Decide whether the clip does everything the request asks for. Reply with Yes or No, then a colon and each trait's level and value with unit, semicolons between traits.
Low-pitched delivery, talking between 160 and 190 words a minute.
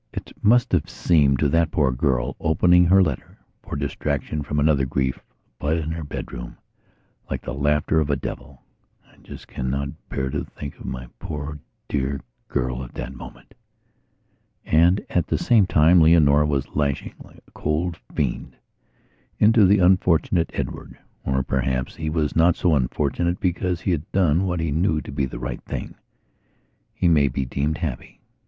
Yes: very low, 75 Hz; average, 170 wpm